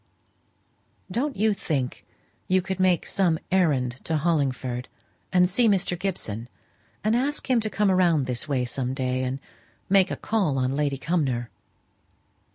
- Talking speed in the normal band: Yes, average, 150 wpm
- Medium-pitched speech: Yes, medium, 165 Hz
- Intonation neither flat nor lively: No, wide, 6.8 semitones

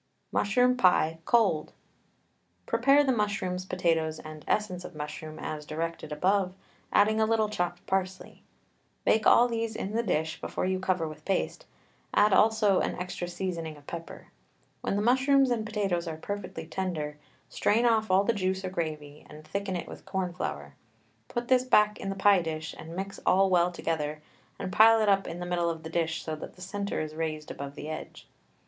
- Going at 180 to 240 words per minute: Yes, average, 185 wpm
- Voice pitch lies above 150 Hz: Yes, medium, 185 Hz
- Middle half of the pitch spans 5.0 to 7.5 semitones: No, average, 4.5 semitones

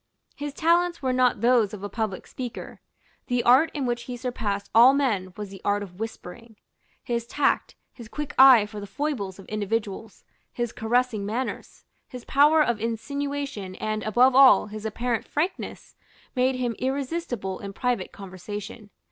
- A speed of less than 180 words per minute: Yes, average, 160 wpm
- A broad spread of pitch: No, average, 4.0 semitones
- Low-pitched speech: No, high, 235 Hz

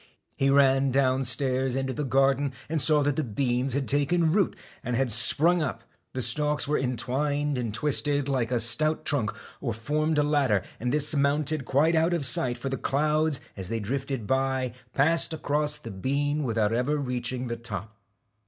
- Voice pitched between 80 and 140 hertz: Yes, low, 135 Hz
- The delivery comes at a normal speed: Yes, average, 180 wpm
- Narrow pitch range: No, average, 3.1 semitones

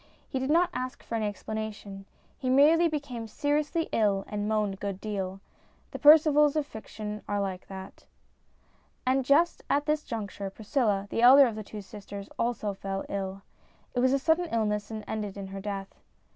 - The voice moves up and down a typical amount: No, wide, 5.8 semitones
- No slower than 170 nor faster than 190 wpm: Yes, average, 180 wpm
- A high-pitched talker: Yes, high, 220 Hz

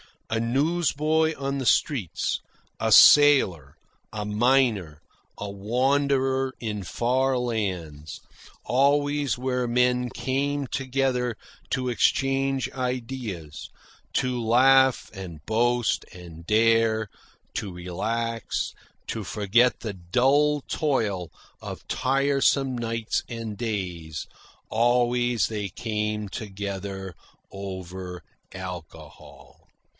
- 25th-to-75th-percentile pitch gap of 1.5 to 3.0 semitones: No, average, 5.2 semitones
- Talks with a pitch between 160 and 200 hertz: No, low, 115 Hz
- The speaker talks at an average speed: No, slow, 90 wpm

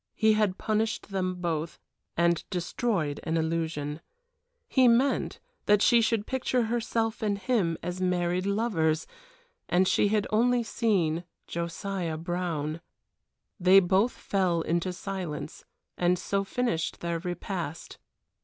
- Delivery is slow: Yes, slow, 125 wpm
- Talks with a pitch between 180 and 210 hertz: Yes, medium, 185 Hz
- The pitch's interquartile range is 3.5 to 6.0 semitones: Yes, average, 4.3 semitones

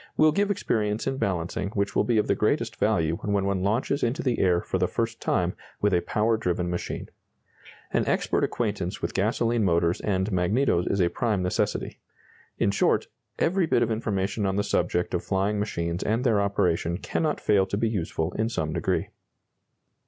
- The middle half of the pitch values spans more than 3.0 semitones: Yes, average, 4.1 semitones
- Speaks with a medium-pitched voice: No, low, 100 Hz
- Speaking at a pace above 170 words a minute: Yes, average, 185 wpm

